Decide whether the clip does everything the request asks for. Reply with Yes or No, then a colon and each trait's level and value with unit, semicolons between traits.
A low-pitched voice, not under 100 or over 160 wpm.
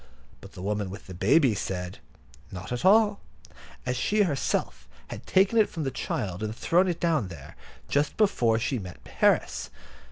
No: low, 125 Hz; average, 170 wpm